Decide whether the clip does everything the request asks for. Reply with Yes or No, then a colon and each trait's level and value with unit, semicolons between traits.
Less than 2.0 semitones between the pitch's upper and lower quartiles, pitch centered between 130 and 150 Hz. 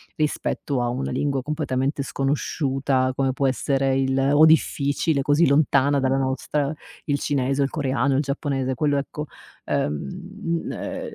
Yes: narrow, 1.6 semitones; medium, 140 Hz